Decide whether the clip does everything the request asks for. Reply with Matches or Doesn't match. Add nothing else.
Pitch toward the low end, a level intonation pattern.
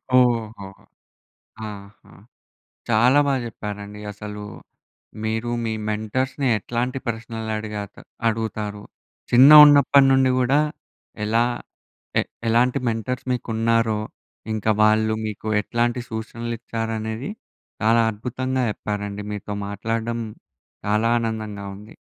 Matches